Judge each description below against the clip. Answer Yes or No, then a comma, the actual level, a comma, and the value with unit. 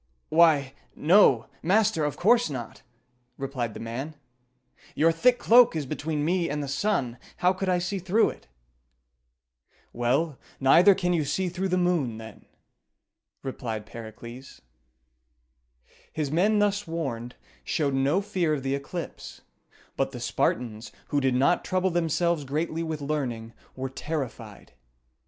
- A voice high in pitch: No, medium, 155 Hz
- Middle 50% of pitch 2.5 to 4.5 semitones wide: No, average, 5.2 semitones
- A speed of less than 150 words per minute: Yes, average, 140 wpm